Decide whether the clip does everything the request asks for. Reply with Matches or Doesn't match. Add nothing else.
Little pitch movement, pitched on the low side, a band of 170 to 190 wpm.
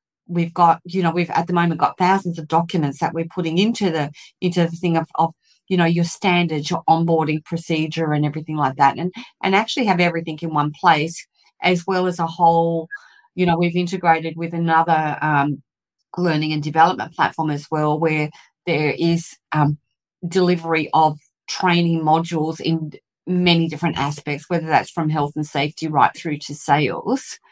Doesn't match